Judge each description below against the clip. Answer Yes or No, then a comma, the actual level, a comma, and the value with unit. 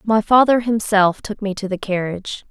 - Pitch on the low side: No, high, 205 Hz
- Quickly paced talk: No, average, 190 wpm